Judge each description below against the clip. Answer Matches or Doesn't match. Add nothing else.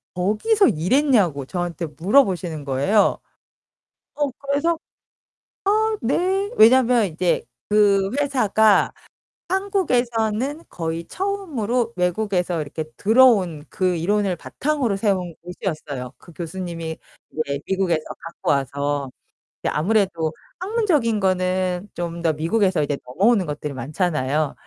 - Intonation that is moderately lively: Doesn't match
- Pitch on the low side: Doesn't match